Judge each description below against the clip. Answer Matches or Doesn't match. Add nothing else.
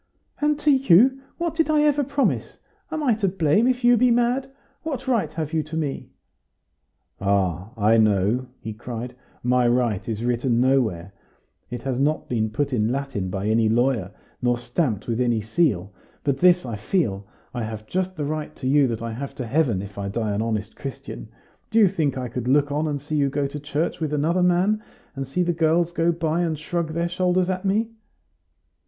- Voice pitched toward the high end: Doesn't match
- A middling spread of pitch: Doesn't match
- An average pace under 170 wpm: Doesn't match